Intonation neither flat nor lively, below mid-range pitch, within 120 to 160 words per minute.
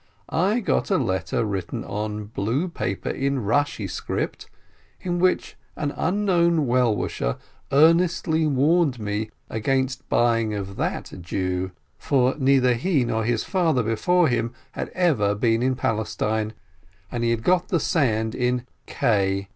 No: wide, 6.7 semitones; low, 125 Hz; average, 140 wpm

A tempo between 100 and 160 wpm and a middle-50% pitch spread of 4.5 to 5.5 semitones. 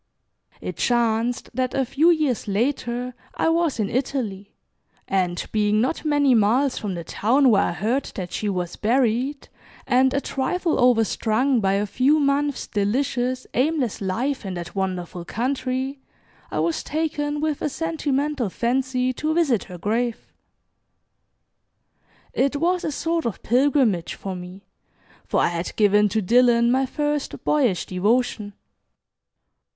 Yes: average, 140 wpm; average, 5.2 semitones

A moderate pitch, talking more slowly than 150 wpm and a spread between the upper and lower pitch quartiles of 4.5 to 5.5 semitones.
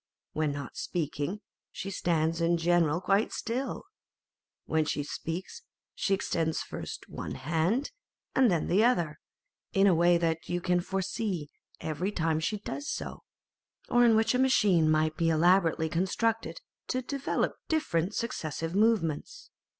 Yes: medium, 175 Hz; average, 140 wpm; average, 5.0 semitones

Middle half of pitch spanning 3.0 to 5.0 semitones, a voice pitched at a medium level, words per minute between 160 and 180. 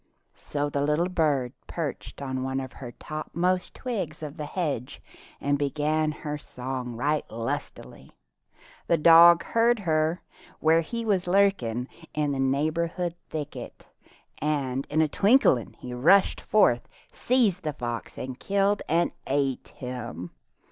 No: average, 4.6 semitones; medium, 150 Hz; slow, 135 wpm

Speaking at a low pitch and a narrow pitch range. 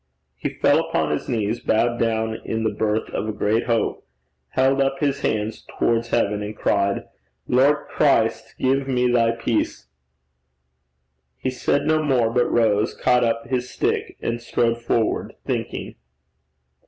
Yes: low, 115 Hz; narrow, 2.3 semitones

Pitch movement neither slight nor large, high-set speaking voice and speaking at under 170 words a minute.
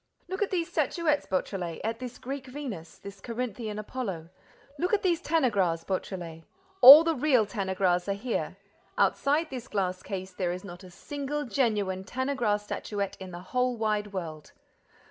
No: wide, 6.2 semitones; high, 215 Hz; average, 160 wpm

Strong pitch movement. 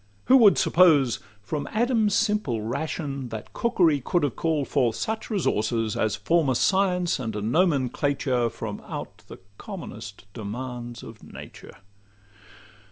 Yes: wide, 7.5 semitones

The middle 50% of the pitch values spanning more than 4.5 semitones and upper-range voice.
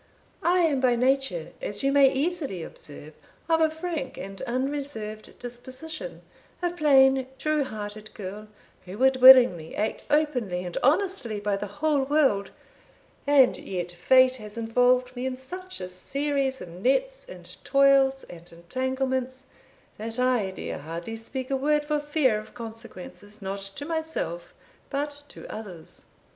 Yes: wide, 5.4 semitones; very high, 260 Hz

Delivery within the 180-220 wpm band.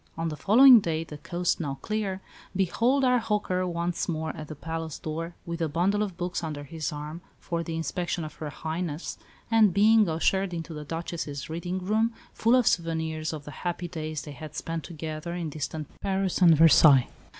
Yes: average, 190 wpm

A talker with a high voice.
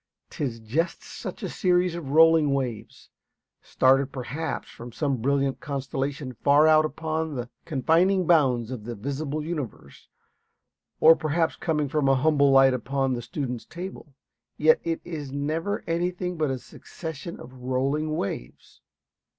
No: medium, 145 Hz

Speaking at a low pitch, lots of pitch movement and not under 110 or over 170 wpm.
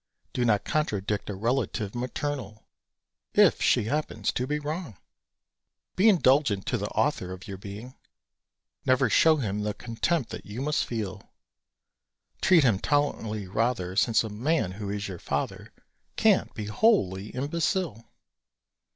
Yes: low, 115 Hz; wide, 6.2 semitones; average, 140 wpm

